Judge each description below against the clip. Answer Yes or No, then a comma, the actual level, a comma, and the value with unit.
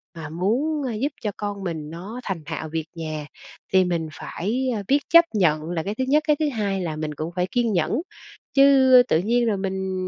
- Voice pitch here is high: Yes, high, 195 Hz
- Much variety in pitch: Yes, wide, 7.0 semitones